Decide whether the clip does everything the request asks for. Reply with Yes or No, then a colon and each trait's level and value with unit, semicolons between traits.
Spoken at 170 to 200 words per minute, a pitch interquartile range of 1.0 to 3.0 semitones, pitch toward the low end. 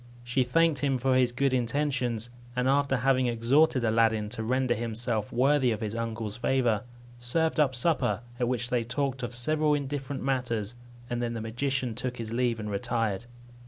Yes: average, 175 wpm; narrow, 2.6 semitones; low, 125 Hz